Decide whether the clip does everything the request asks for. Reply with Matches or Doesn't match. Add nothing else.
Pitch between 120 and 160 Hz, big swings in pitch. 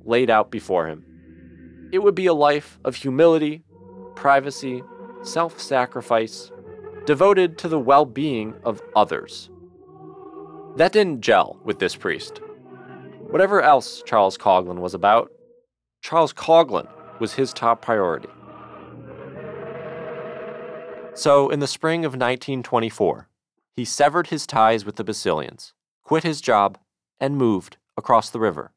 Matches